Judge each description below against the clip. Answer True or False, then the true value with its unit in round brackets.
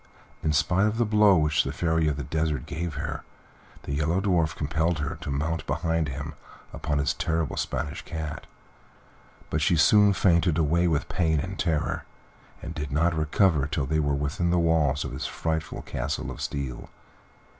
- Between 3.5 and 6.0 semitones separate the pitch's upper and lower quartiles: False (2.7 semitones)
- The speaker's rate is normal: True (175 wpm)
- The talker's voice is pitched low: True (80 Hz)